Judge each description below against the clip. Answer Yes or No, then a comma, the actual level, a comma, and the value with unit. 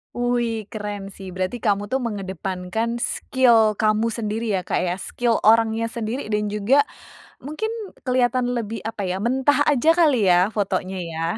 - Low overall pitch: No, high, 220 Hz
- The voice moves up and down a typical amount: Yes, average, 3.5 semitones